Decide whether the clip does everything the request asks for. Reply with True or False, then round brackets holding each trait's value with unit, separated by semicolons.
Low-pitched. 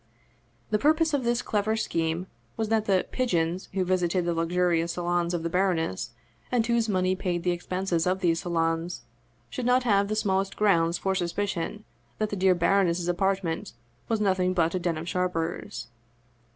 False (185 Hz)